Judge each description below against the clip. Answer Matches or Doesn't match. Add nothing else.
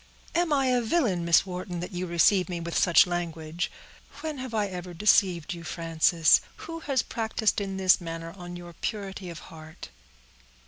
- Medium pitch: Matches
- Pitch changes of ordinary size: Matches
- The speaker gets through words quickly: Doesn't match